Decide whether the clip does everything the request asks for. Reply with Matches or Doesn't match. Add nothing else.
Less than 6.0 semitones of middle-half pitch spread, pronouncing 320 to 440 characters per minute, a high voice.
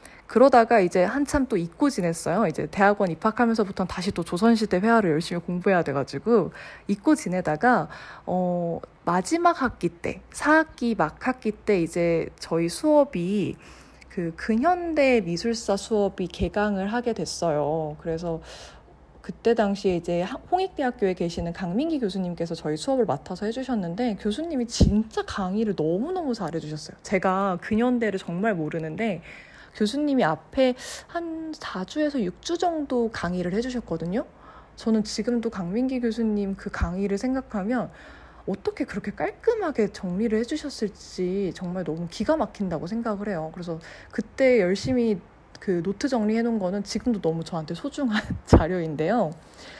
Matches